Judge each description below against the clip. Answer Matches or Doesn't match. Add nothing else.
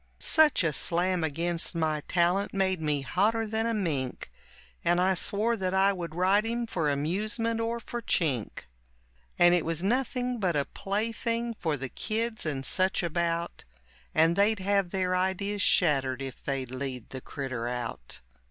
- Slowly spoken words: Doesn't match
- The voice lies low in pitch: Doesn't match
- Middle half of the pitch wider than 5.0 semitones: Matches